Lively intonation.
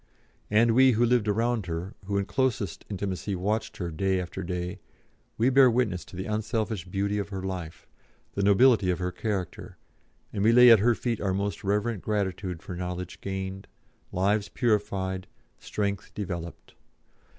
No: average, 3.0 semitones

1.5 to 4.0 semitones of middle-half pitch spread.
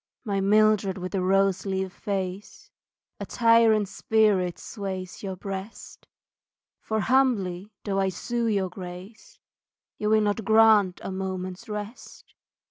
Yes: narrow, 2.5 semitones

